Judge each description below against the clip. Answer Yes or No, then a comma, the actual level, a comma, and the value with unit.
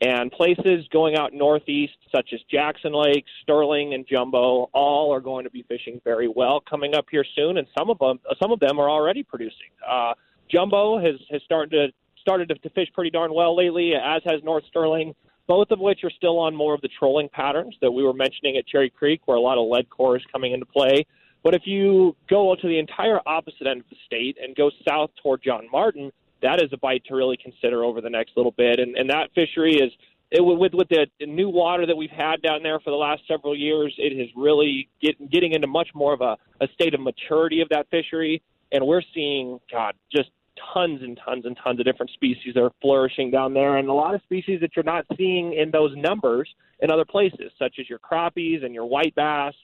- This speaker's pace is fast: Yes, fast, 225 wpm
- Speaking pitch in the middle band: Yes, medium, 150 Hz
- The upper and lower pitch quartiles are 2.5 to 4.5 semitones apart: Yes, average, 3.8 semitones